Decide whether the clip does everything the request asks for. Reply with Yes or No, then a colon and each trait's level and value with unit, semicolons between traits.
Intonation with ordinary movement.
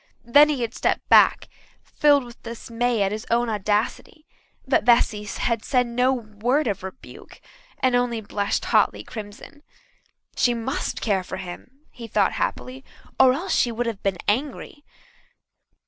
Yes: average, 3.5 semitones